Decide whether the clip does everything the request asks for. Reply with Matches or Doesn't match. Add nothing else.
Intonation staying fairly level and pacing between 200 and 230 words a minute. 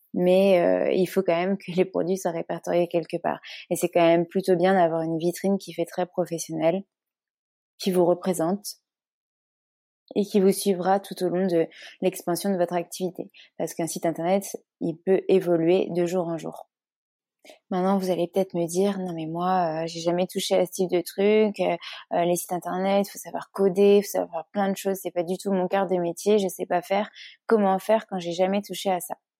Matches